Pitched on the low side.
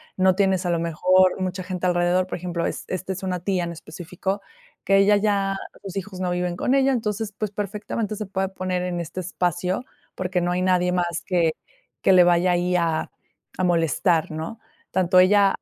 No: medium, 185 Hz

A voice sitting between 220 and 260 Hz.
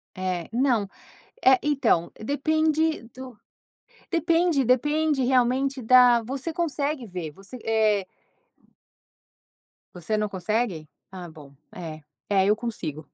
Yes: high, 240 Hz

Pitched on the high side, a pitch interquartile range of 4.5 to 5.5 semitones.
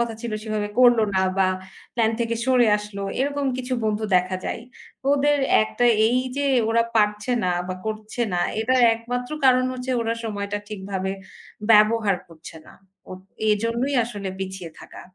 No: high, 225 Hz; average, 3.6 semitones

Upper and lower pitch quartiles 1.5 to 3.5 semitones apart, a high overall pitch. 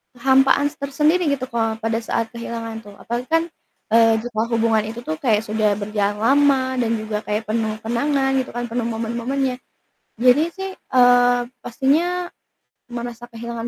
Yes: average, 3.1 semitones; high, 235 Hz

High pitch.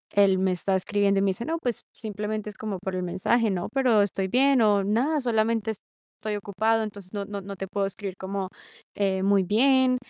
Yes: high, 205 Hz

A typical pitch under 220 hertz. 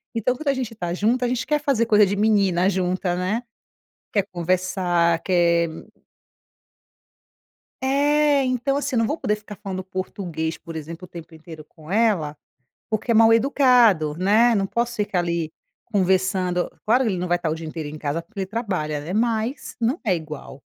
Yes: high, 190 Hz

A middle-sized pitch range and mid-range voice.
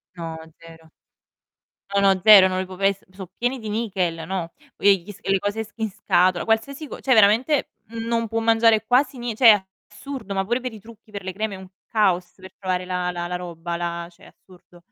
No: average, 3.8 semitones; high, 200 Hz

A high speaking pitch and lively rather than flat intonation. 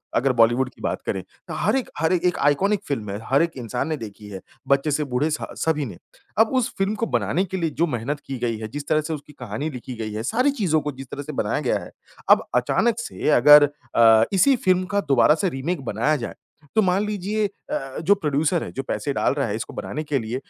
No: medium, 150 Hz; wide, 6.5 semitones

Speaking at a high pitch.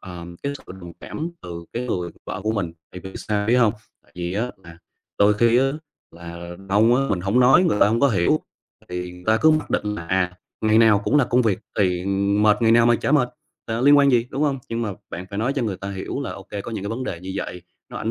No: low, 105 Hz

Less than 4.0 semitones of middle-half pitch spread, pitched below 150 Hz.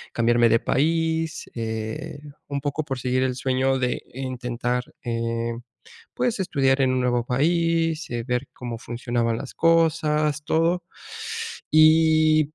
No: average, 4.5 semitones; low, 135 Hz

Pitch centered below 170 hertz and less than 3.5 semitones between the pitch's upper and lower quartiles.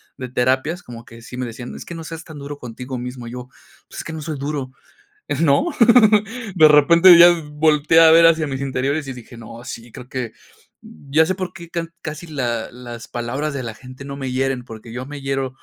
No: low, 135 Hz; average, 4.1 semitones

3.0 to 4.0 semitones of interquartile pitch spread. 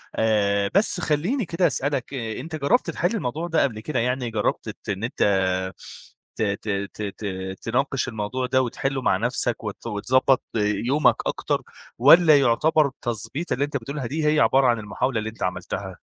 No: average, 5.2 semitones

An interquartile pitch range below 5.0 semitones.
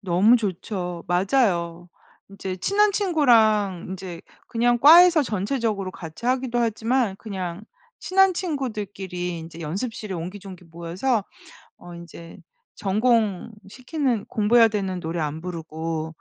No: wide, 5.4 semitones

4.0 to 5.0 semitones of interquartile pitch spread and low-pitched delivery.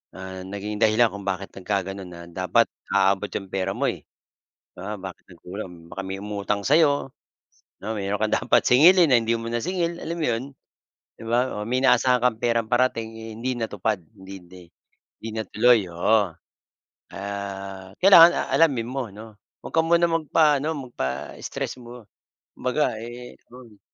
Yes: average, 4.5 semitones; low, 110 Hz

